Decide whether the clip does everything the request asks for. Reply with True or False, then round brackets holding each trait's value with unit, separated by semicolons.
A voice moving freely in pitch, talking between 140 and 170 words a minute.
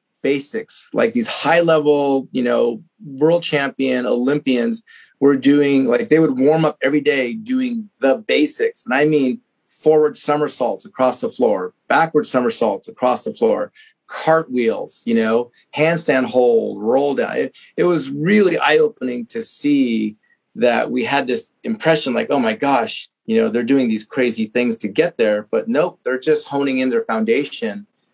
True (8.6 semitones; 165 wpm)